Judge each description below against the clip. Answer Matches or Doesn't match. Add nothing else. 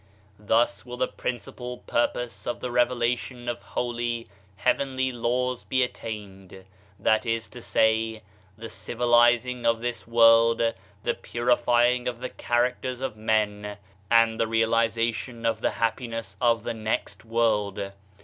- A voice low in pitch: Matches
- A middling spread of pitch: Doesn't match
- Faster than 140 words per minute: Doesn't match